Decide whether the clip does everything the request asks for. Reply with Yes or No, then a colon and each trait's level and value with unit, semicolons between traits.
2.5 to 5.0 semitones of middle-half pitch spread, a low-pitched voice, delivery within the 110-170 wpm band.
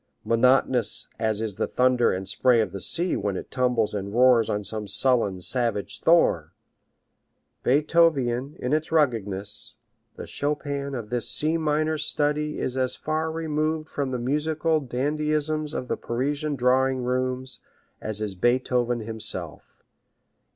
Yes: average, 4.7 semitones; low, 130 Hz; average, 145 wpm